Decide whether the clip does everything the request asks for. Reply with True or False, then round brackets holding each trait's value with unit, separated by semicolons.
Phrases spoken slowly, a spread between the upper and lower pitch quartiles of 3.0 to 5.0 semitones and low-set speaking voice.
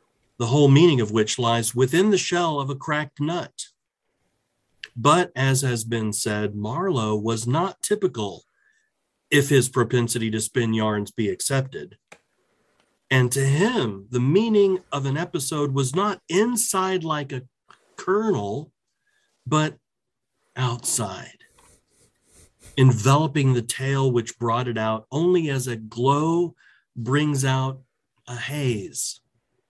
True (125 wpm; 4.4 semitones; 130 Hz)